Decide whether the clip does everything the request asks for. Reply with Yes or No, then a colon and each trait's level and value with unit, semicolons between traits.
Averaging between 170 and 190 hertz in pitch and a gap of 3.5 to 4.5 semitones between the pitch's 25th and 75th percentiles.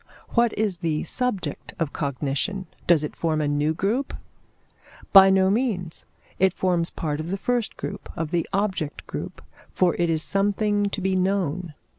Yes: medium, 185 Hz; average, 3.9 semitones